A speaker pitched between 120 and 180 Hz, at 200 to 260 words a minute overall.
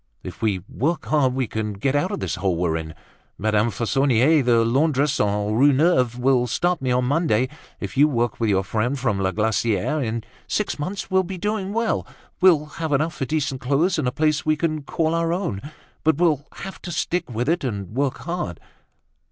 Yes: low, 135 Hz; fast, 205 wpm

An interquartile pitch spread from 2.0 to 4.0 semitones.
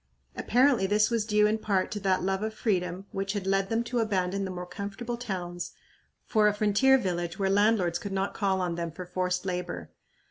Yes: average, 2.7 semitones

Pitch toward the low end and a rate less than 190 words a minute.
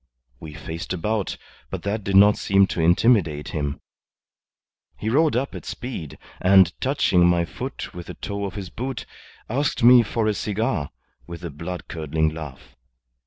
Yes: very low, 95 Hz; average, 165 wpm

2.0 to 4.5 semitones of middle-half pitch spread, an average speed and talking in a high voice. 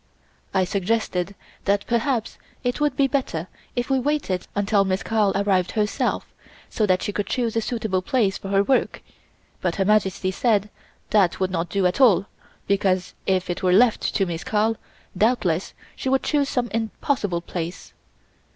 Yes: average, 3.8 semitones; average, 170 wpm; high, 200 Hz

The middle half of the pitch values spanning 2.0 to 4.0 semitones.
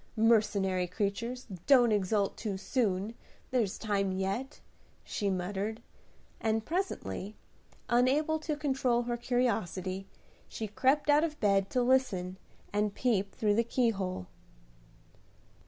No: average, 4.4 semitones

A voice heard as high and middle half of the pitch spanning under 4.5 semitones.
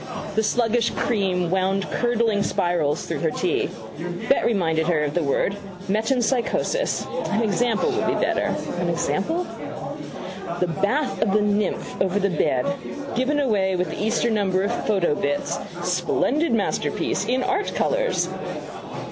No: high, 205 Hz; average, 4.8 semitones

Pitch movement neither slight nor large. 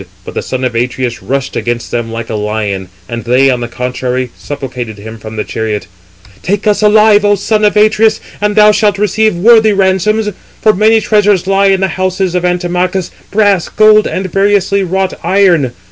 No: wide, 8.8 semitones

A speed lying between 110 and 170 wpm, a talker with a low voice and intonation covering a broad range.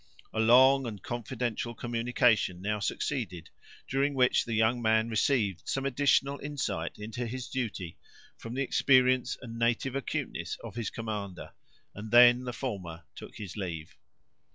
No: average, 145 wpm; low, 120 Hz; average, 3.4 semitones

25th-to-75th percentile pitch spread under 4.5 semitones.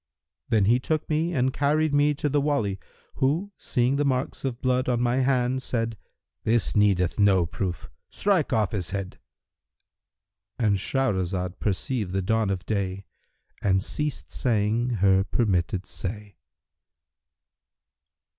No: wide, 5.4 semitones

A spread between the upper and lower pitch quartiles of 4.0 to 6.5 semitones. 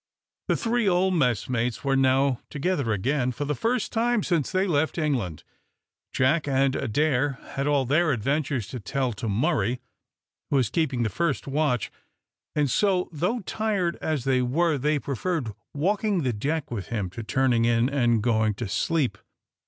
Yes: average, 5.2 semitones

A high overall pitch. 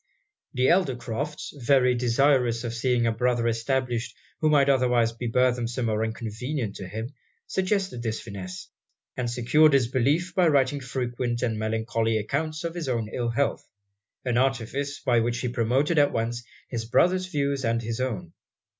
No: low, 125 Hz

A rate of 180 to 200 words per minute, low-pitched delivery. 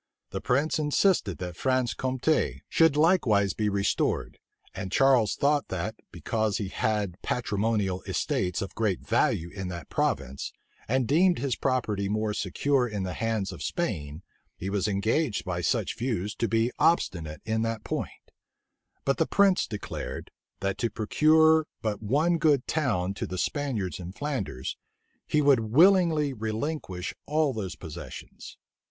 No: average, 145 wpm; low, 110 Hz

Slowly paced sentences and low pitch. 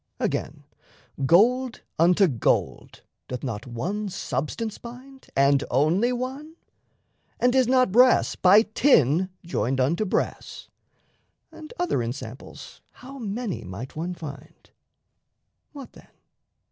No: slow, 110 wpm; high, 190 Hz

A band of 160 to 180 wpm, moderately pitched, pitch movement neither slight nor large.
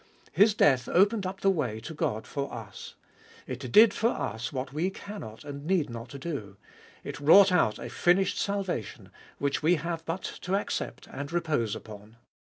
No: average, 175 wpm; medium, 150 Hz; wide, 7.6 semitones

